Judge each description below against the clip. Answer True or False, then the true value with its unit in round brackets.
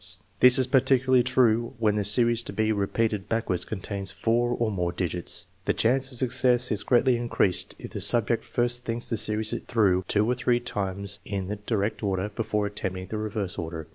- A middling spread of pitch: True (3.3 semitones)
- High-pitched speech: False (110 Hz)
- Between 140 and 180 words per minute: False (195 wpm)